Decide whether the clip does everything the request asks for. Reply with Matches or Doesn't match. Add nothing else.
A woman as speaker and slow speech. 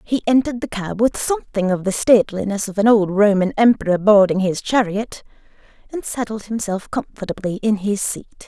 Doesn't match